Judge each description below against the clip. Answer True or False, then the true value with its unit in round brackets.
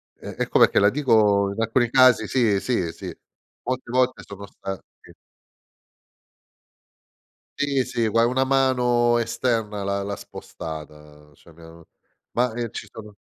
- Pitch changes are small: False (3.8 semitones)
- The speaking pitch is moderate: False (115 Hz)